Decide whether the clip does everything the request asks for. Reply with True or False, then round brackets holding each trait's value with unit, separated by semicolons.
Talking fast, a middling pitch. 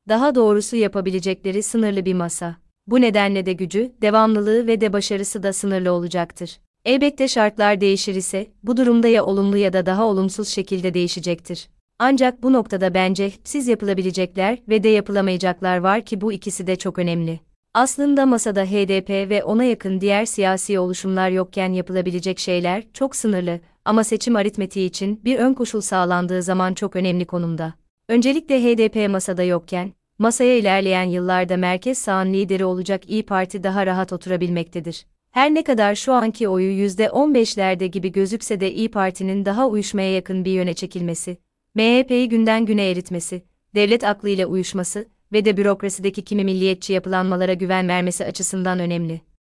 False (150 wpm; 195 Hz)